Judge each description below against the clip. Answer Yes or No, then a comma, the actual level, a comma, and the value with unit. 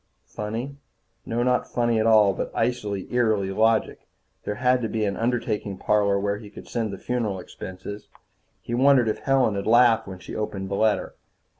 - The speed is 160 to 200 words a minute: Yes, average, 180 wpm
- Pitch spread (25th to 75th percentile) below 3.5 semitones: Yes, average, 3.0 semitones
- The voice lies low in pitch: Yes, low, 110 Hz